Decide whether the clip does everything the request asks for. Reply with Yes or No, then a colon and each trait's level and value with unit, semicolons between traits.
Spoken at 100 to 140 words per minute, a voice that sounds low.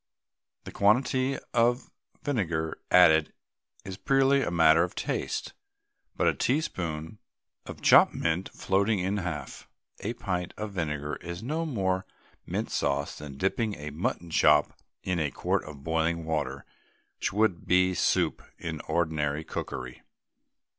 Yes: slow, 135 wpm; very low, 90 Hz